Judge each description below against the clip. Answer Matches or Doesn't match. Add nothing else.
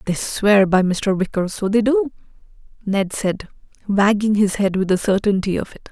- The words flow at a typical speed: Matches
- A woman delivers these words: Matches